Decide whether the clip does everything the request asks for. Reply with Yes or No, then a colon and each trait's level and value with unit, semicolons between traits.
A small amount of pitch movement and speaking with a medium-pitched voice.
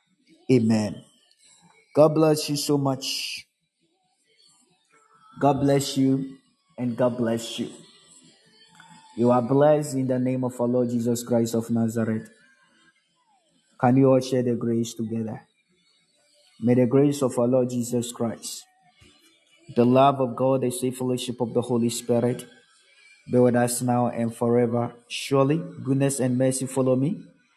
No: narrow, 2.0 semitones; low, 125 Hz